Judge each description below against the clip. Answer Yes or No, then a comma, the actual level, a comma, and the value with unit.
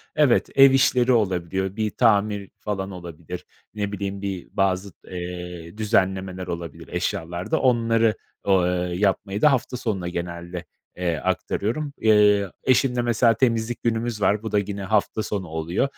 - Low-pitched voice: Yes, low, 100 Hz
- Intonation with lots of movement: No, average, 4.0 semitones